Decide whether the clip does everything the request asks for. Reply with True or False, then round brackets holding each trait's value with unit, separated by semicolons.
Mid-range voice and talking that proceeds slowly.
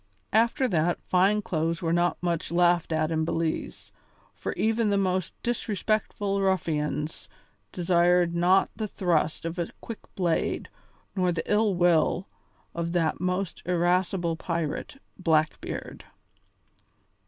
True (175 Hz; 120 wpm)